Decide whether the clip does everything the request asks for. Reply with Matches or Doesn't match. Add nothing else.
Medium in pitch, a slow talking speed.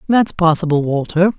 Matches